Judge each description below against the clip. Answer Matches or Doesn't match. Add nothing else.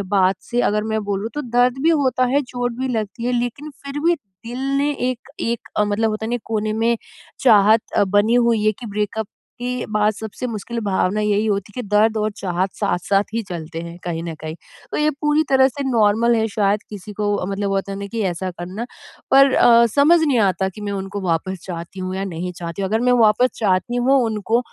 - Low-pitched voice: Doesn't match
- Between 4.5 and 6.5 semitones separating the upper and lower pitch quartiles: Doesn't match